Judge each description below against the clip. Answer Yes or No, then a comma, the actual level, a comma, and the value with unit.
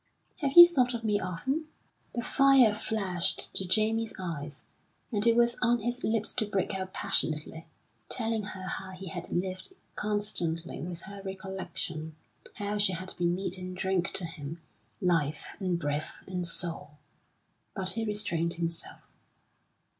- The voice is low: No, high, 190 Hz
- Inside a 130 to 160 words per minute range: Yes, average, 150 wpm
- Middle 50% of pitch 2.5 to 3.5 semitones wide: No, average, 4.0 semitones